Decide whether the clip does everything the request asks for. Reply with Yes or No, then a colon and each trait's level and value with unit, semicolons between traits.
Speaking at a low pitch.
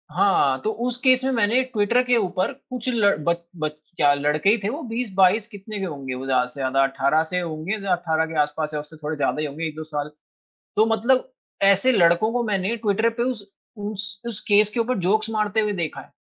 No: high, 195 Hz